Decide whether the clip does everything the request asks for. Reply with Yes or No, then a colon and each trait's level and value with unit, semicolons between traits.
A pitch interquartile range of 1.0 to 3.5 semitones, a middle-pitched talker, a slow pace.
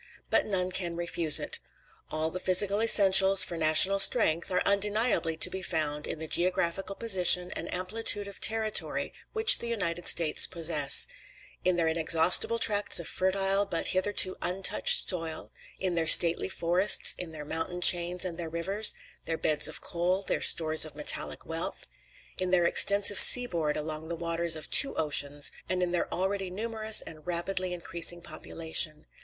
No: average, 3.0 semitones; medium, 175 Hz; average, 165 wpm